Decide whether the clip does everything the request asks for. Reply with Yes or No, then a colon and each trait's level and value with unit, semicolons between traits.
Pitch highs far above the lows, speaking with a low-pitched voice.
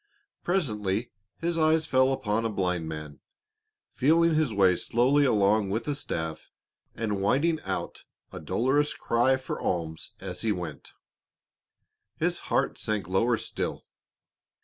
Yes: wide, 6.7 semitones; low, 115 Hz